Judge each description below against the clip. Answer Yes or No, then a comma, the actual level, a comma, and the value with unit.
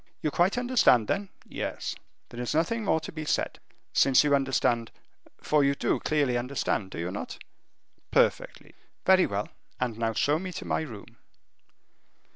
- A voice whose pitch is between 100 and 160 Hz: Yes, medium, 140 Hz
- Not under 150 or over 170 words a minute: Yes, average, 160 wpm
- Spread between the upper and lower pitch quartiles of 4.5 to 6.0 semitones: Yes, wide, 5.4 semitones